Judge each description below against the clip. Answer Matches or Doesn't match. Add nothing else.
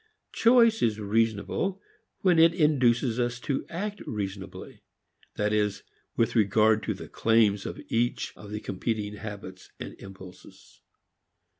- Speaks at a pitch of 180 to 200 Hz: Doesn't match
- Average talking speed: Doesn't match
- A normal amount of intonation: Matches